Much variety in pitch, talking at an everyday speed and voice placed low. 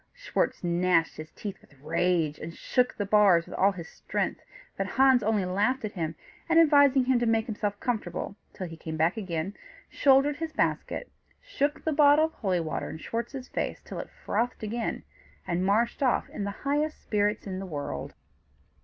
No: wide, 6.9 semitones; average, 185 wpm; high, 210 Hz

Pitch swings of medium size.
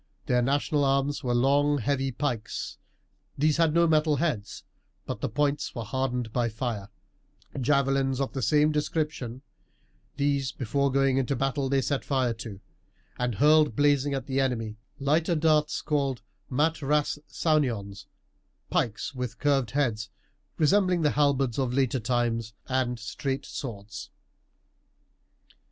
Yes: average, 3.1 semitones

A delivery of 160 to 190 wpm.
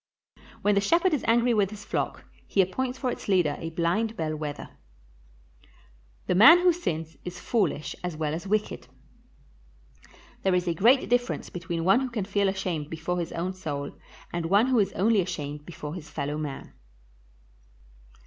Yes: average, 170 wpm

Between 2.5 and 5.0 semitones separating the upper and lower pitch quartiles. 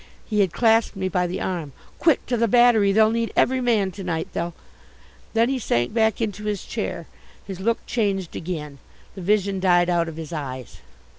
Yes: average, 4.5 semitones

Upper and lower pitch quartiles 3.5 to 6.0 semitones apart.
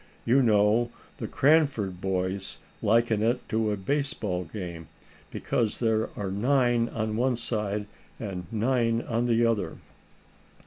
No: average, 2.9 semitones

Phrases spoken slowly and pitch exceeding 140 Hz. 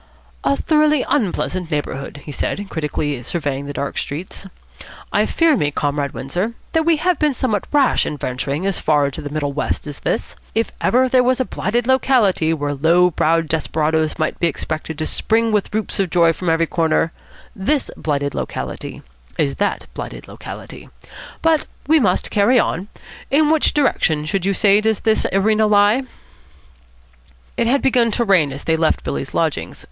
No: average, 175 wpm; medium, 185 Hz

